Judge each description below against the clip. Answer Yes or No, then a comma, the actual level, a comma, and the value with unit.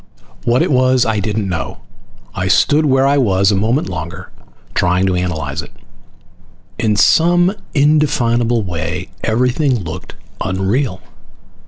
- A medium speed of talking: No, slow, 130 wpm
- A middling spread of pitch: No, wide, 5.9 semitones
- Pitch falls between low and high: No, low, 110 Hz